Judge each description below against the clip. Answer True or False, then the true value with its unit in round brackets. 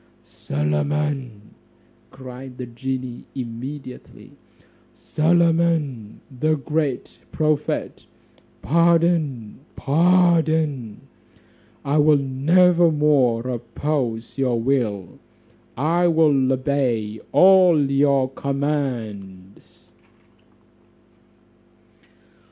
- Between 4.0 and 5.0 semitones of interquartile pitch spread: True (4.3 semitones)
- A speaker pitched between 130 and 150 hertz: True (140 Hz)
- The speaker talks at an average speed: False (65 wpm)